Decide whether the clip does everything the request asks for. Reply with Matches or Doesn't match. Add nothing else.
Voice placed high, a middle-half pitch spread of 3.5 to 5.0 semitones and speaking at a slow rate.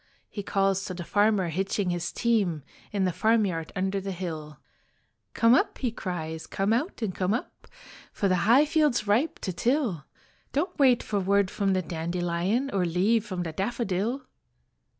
Doesn't match